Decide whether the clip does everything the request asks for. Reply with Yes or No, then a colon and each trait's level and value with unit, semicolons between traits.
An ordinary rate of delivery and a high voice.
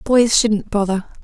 Yes: average, 145 wpm; high, 215 Hz